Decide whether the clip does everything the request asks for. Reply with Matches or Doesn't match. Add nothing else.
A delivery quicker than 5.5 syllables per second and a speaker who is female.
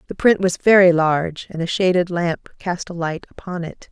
Doesn't match